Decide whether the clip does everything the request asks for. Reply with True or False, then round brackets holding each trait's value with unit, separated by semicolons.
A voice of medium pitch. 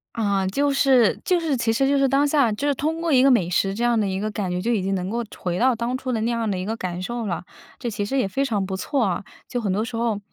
False (230 Hz)